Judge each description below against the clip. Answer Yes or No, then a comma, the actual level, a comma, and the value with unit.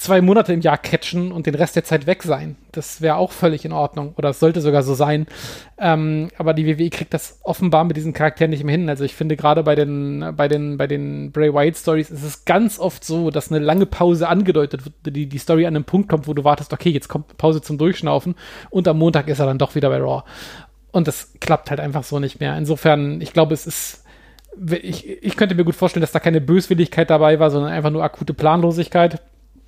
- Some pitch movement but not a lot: No, narrow, 2.3 semitones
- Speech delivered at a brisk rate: Yes, fast, 235 wpm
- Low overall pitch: No, medium, 155 Hz